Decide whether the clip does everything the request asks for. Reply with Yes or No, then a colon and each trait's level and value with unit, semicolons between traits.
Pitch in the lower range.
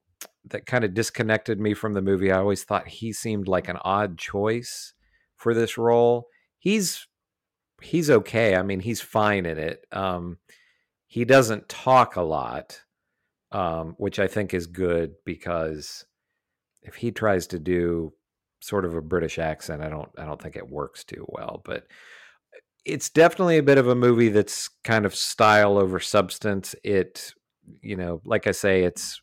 Yes: low, 100 Hz